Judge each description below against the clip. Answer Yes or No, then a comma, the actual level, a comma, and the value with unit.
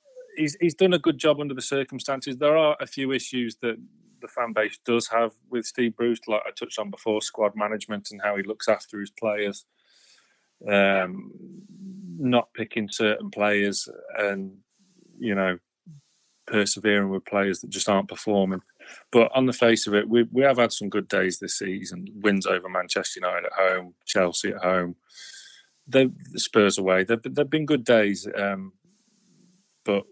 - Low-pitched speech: Yes, low, 115 Hz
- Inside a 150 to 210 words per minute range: Yes, average, 175 wpm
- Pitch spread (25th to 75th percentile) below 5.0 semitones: No, wide, 5.5 semitones